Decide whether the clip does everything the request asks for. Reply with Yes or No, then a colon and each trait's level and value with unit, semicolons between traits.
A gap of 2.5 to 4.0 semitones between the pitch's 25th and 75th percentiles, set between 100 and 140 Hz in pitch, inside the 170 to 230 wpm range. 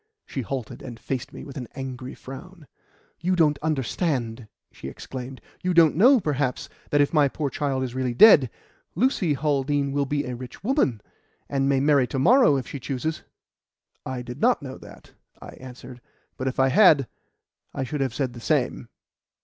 Yes: average, 2.9 semitones; low, 135 Hz; average, 180 wpm